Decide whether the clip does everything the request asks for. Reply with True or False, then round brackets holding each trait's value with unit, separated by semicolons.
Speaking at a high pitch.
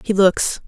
True (195 Hz)